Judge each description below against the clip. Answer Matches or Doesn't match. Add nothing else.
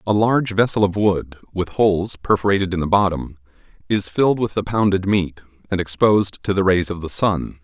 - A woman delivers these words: Doesn't match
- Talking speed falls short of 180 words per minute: Doesn't match